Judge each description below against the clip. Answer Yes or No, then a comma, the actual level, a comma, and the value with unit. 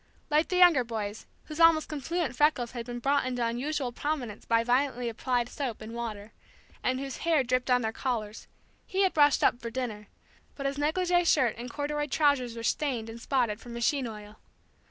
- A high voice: Yes, very high, 255 Hz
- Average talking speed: Yes, average, 190 wpm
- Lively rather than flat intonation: No, average, 4.1 semitones